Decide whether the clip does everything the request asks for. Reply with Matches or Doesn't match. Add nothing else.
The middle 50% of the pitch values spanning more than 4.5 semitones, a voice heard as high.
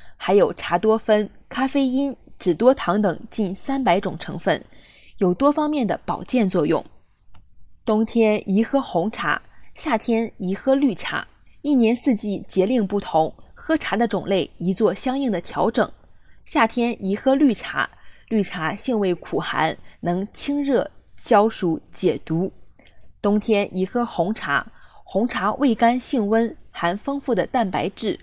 Matches